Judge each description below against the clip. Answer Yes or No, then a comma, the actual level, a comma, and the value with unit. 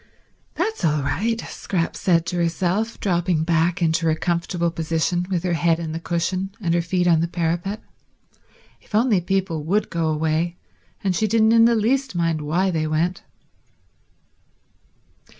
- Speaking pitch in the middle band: Yes, medium, 175 Hz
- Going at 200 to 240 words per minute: No, average, 155 wpm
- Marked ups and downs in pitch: No, average, 2.8 semitones